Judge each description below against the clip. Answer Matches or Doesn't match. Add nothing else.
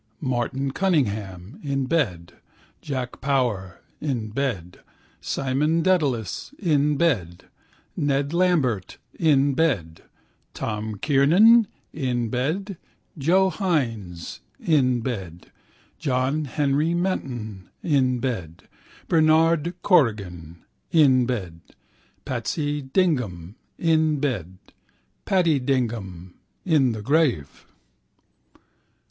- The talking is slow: Matches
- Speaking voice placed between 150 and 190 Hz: Doesn't match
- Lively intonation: Matches